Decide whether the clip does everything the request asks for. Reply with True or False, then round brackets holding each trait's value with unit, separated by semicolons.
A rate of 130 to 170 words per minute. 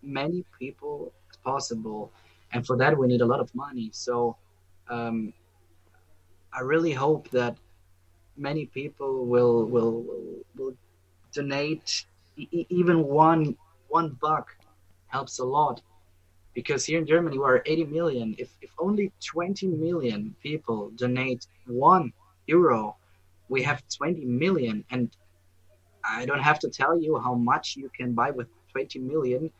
True (140 wpm)